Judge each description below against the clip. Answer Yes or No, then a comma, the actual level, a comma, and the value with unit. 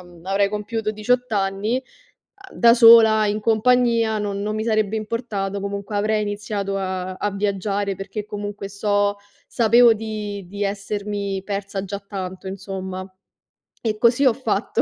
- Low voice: No, high, 205 Hz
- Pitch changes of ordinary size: No, narrow, 1.9 semitones